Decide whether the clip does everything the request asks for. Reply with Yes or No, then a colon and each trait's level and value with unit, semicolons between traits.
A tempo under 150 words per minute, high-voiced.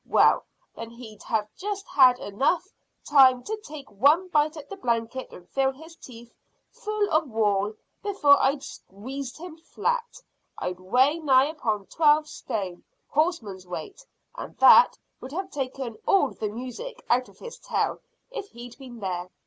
No: average, 155 wpm; very high, 265 Hz